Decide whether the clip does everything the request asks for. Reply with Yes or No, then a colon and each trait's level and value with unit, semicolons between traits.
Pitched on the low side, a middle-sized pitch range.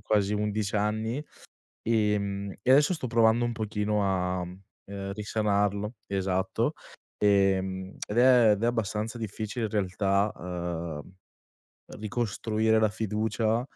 No: low, 105 Hz; narrow, 2.2 semitones